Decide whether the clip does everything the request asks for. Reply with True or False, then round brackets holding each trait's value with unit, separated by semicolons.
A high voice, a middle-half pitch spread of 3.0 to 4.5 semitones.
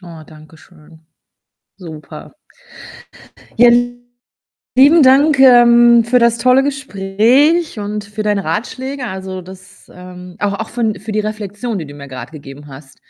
False (210 Hz; 5.2 semitones)